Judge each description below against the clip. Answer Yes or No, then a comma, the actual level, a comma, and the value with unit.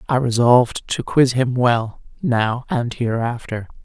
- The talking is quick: No, average, 140 wpm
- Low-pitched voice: Yes, low, 125 Hz